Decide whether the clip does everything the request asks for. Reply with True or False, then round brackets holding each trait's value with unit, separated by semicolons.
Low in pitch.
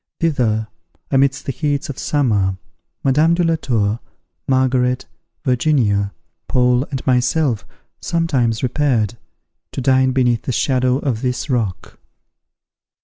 True (130 Hz)